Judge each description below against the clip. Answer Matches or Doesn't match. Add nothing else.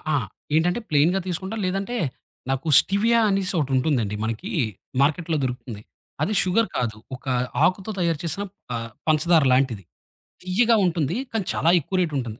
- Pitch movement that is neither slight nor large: Doesn't match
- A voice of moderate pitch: Matches